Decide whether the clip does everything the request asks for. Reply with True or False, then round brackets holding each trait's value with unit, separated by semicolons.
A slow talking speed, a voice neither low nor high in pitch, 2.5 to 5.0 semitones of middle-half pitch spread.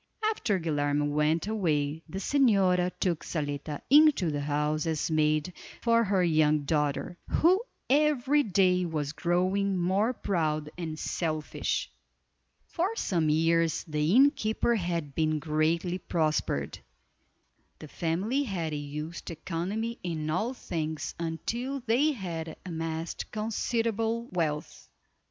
False (115 wpm; 170 Hz; 5.6 semitones)